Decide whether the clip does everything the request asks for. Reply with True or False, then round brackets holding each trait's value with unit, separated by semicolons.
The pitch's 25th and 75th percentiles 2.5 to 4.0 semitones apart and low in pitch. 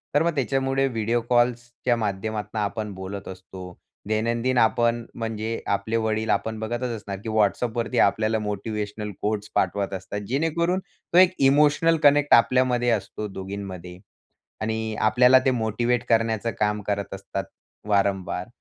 True (3.1 semitones; 110 Hz)